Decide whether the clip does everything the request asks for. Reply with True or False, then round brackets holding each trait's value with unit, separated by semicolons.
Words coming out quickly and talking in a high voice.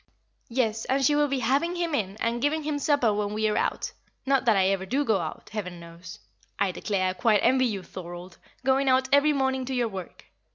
True (220 wpm; 230 Hz)